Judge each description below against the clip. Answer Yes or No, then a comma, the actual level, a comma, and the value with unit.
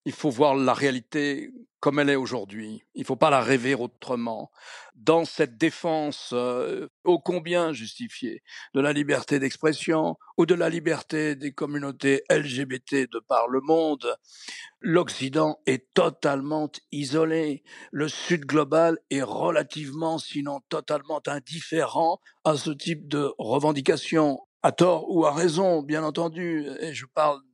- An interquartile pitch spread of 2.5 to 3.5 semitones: Yes, average, 2.9 semitones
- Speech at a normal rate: No, slow, 140 wpm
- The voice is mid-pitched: Yes, medium, 150 Hz